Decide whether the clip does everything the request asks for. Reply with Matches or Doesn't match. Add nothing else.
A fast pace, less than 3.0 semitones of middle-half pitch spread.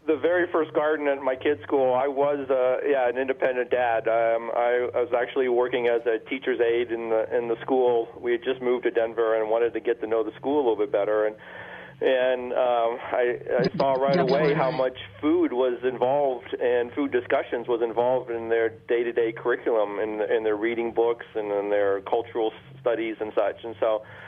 Matches